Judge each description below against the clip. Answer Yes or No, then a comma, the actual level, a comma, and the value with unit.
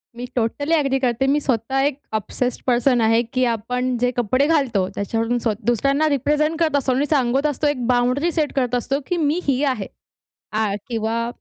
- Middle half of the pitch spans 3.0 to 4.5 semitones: Yes, average, 3.4 semitones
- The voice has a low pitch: No, very high, 255 Hz